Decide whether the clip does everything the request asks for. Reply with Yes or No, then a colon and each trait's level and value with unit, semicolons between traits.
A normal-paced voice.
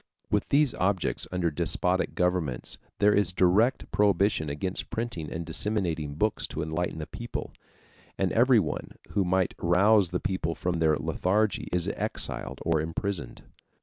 Yes: average, 145 wpm